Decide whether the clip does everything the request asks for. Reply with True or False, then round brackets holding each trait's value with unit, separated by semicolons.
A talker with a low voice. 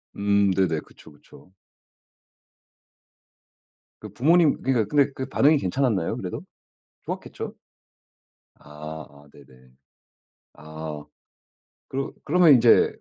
True (100 Hz)